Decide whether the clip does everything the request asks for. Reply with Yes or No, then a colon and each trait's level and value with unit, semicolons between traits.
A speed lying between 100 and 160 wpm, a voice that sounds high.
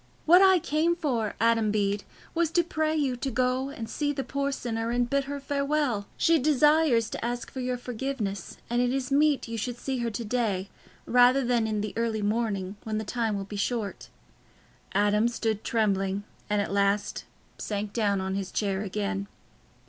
No: average, 185 wpm; high, 235 Hz